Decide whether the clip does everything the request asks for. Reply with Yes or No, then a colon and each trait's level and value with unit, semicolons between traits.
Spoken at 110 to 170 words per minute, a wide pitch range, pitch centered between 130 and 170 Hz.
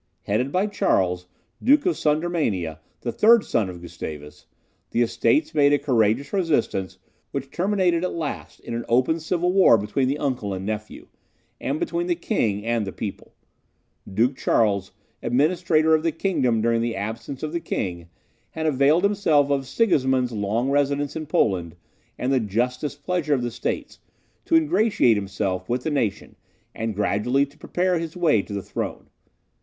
Yes: average, 165 wpm; wide, 7.1 semitones; low, 135 Hz